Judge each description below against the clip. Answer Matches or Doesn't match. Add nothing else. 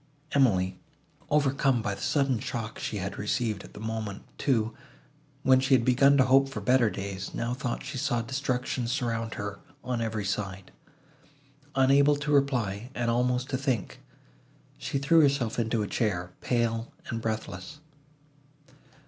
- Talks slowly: Doesn't match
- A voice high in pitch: Doesn't match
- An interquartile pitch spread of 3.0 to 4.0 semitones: Matches